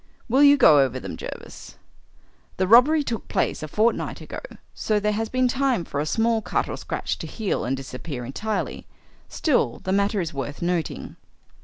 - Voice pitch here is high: Yes, high, 205 Hz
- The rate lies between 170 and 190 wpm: Yes, average, 180 wpm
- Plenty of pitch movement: Yes, wide, 7.9 semitones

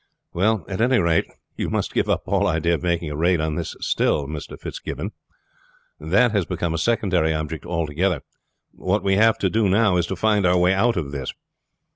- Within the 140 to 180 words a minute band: No, average, 200 wpm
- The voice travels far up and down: No, average, 3.9 semitones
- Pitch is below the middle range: Yes, very low, 90 Hz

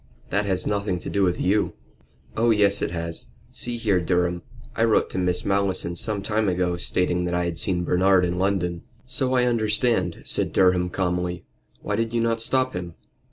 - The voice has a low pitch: Yes, very low, 95 Hz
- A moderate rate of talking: Yes, average, 190 wpm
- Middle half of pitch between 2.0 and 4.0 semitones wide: Yes, average, 3.4 semitones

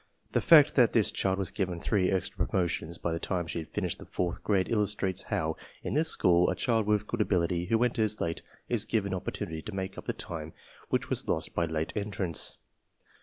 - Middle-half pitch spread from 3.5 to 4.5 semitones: Yes, average, 3.8 semitones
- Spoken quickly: Yes, fast, 210 wpm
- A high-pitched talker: No, very low, 95 Hz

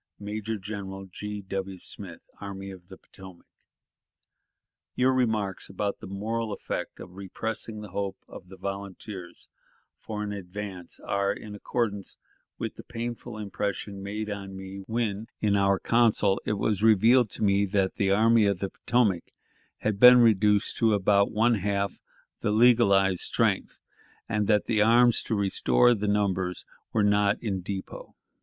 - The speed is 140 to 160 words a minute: Yes, average, 155 wpm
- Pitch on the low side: Yes, low, 100 Hz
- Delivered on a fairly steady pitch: Yes, narrow, 2.0 semitones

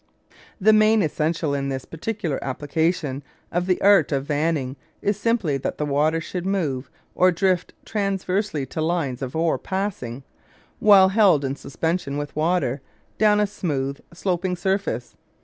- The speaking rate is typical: Yes, average, 150 wpm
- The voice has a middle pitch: Yes, medium, 165 Hz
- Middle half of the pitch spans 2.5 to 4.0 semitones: No, average, 5.3 semitones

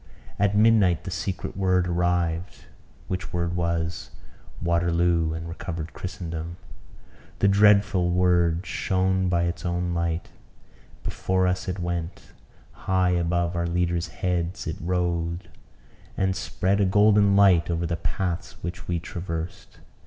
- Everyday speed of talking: No, slow, 130 wpm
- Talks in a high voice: No, very low, 90 Hz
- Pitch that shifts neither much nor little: No, narrow, 1.7 semitones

